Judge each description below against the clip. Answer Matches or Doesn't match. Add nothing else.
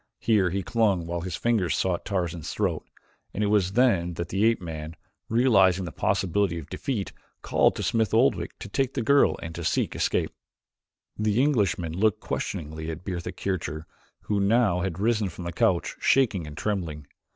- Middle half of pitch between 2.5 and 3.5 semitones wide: Doesn't match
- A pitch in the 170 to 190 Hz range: Doesn't match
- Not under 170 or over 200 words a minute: Matches